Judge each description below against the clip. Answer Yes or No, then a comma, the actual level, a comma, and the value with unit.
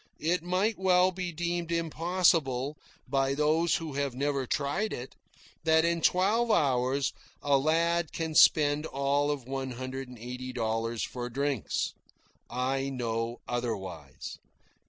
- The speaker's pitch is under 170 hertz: Yes, medium, 140 Hz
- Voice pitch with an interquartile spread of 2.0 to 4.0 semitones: No, average, 4.7 semitones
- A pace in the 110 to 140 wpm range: Yes, slow, 135 wpm